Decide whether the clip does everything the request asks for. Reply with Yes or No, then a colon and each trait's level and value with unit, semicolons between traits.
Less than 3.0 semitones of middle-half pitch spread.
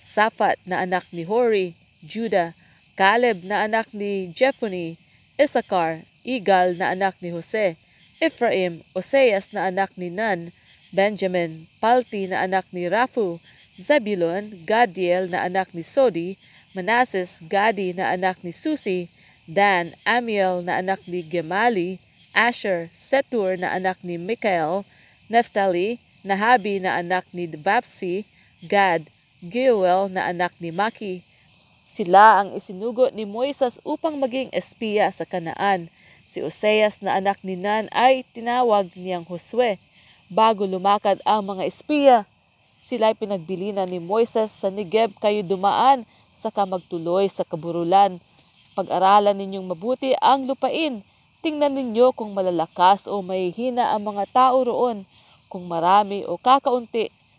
No: average, 3.9 semitones